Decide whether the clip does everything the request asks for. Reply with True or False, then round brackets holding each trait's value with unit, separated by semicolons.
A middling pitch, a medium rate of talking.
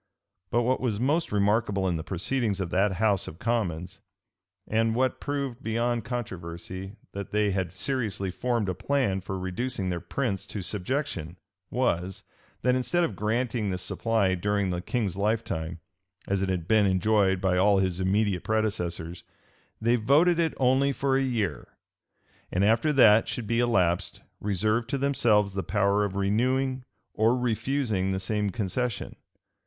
False (105 Hz; 155 wpm)